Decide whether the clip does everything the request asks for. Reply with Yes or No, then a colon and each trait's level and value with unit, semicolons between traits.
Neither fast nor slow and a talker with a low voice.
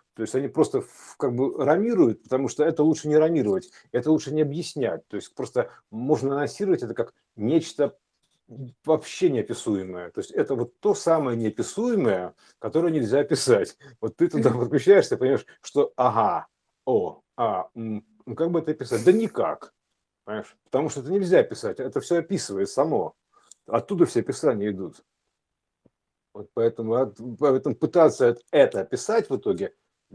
No: average, 150 wpm; medium, 155 Hz